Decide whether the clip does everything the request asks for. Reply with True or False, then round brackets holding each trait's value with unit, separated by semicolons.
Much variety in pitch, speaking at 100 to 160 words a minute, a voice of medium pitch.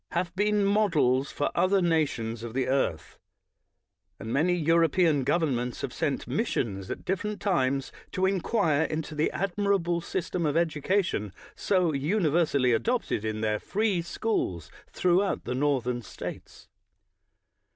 True (6.4 semitones; 140 wpm; 160 Hz)